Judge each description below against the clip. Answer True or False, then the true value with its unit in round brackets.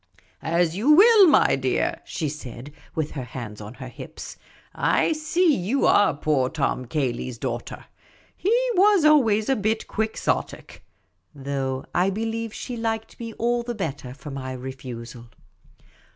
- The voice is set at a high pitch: False (170 Hz)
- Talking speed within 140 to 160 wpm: True (150 wpm)